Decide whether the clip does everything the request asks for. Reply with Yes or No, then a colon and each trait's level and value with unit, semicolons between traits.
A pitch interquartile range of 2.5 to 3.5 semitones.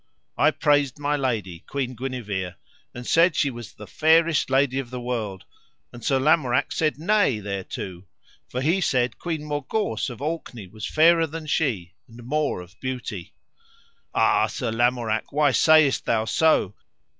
No: average, 5.2 semitones